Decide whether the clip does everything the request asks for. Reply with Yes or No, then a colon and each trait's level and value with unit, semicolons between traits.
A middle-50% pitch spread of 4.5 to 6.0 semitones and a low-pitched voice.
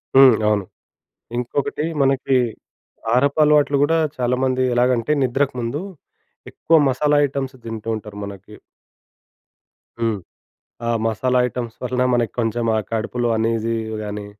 No: average, 2.9 semitones; low, 125 Hz